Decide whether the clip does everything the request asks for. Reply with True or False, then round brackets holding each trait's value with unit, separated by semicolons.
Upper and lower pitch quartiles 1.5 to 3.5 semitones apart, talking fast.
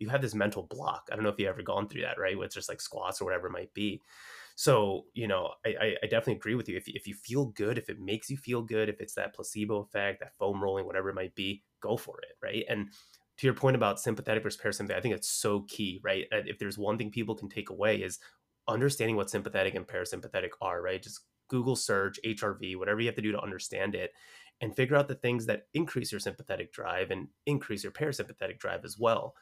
False (4.1 semitones; 245 wpm)